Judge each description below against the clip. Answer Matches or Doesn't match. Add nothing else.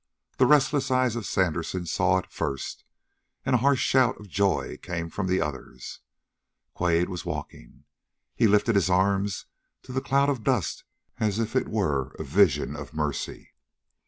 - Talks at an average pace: Matches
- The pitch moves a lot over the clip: Matches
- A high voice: Doesn't match